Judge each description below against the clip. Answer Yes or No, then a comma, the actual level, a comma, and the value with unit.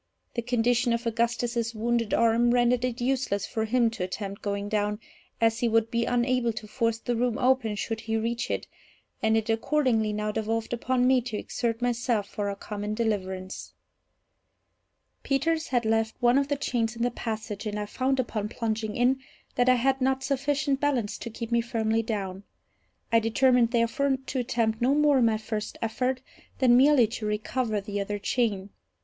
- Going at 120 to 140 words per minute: No, average, 180 wpm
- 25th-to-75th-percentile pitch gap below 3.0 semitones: Yes, narrow, 2.4 semitones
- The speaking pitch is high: Yes, high, 230 Hz